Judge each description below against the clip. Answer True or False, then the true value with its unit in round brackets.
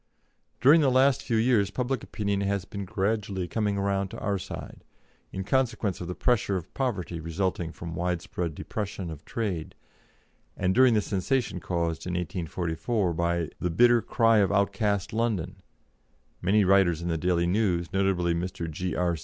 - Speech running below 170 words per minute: True (160 wpm)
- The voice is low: True (95 Hz)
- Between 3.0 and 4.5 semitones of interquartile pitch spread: True (3.7 semitones)